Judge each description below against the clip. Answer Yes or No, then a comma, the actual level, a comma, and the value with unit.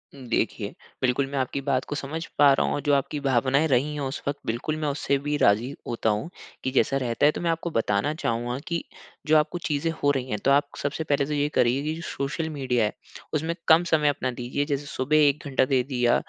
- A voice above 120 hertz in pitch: Yes, medium, 140 Hz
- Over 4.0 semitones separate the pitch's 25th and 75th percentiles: No, average, 2.7 semitones